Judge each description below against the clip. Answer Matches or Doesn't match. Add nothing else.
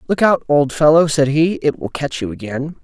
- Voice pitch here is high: Doesn't match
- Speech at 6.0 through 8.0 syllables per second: Doesn't match